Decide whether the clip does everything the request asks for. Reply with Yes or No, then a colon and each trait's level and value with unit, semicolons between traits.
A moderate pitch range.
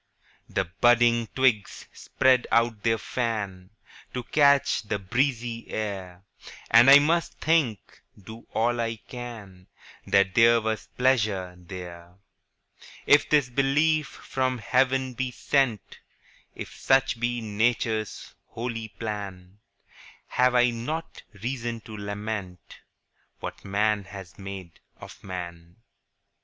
Yes: average, 4.1 semitones